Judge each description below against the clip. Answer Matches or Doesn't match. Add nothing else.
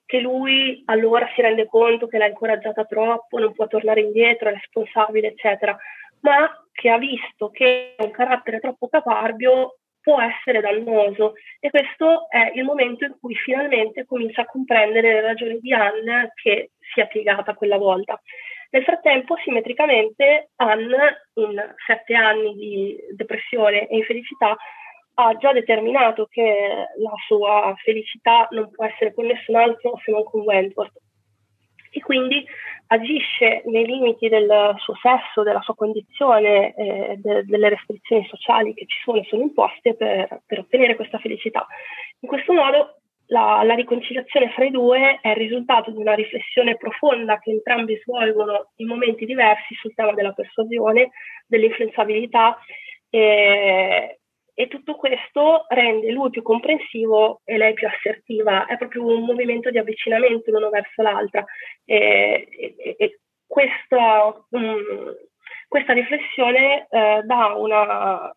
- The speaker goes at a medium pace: Matches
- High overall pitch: Matches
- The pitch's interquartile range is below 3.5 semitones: Matches